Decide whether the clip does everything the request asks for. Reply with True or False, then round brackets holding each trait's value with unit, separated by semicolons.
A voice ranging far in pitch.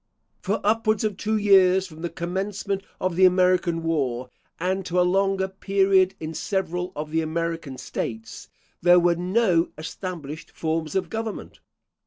False (2.9 semitones)